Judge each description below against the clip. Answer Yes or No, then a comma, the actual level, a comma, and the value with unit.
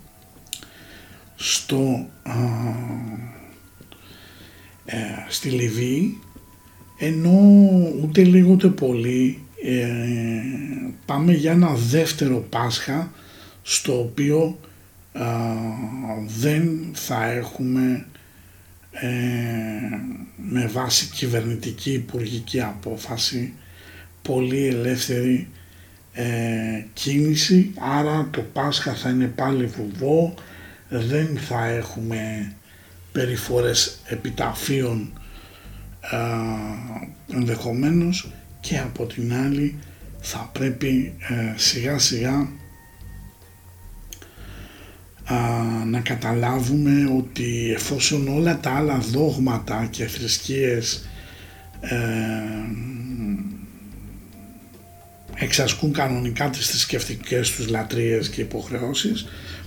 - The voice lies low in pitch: Yes, low, 115 Hz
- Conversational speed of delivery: No, slow, 75 wpm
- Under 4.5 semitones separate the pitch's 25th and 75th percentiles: No, average, 4.8 semitones